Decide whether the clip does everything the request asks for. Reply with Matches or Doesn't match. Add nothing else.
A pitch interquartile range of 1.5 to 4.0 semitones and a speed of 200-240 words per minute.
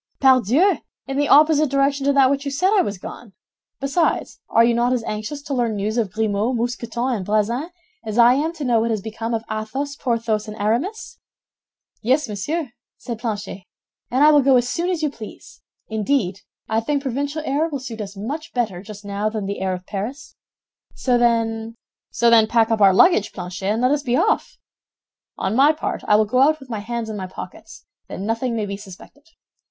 Doesn't match